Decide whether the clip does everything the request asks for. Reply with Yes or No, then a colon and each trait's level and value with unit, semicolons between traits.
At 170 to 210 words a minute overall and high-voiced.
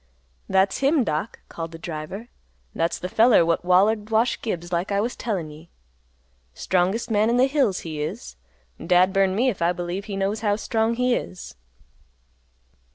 Yes: average, 175 wpm; high, 195 Hz